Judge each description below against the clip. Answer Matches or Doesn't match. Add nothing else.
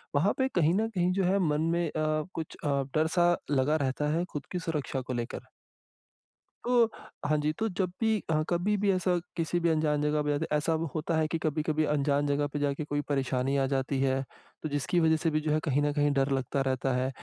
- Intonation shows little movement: Doesn't match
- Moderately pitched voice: Matches